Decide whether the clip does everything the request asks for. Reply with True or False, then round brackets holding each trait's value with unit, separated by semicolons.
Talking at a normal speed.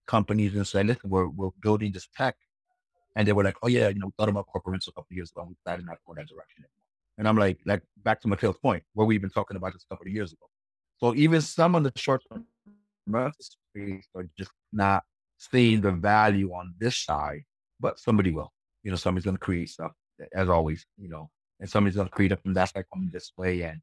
False (245 wpm)